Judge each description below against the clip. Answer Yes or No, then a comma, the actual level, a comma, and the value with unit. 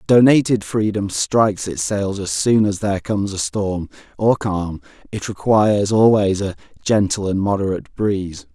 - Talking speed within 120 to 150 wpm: Yes, average, 140 wpm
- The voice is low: Yes, low, 100 Hz